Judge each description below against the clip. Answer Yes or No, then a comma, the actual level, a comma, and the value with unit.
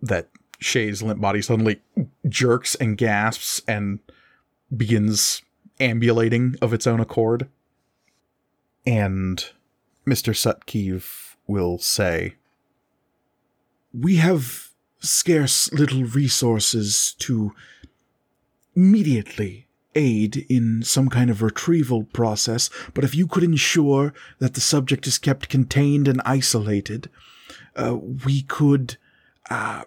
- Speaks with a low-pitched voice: Yes, low, 125 Hz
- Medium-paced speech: No, slow, 100 wpm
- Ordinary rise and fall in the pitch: Yes, average, 3.8 semitones